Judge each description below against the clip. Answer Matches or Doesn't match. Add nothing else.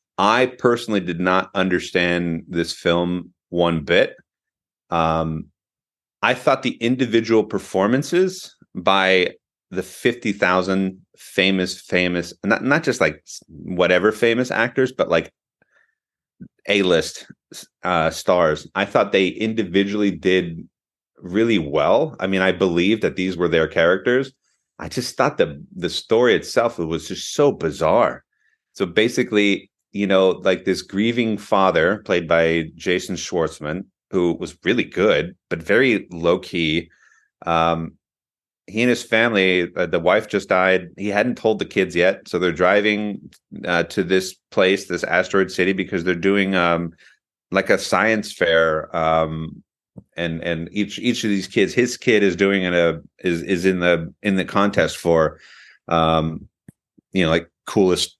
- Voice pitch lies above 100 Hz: Doesn't match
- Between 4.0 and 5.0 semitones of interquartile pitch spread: Doesn't match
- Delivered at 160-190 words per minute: Doesn't match